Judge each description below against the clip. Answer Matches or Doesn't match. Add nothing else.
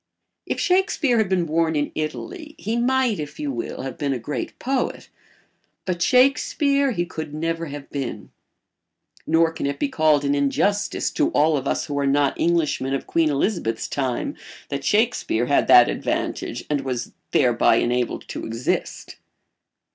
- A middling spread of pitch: Doesn't match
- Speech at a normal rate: Matches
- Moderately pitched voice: Matches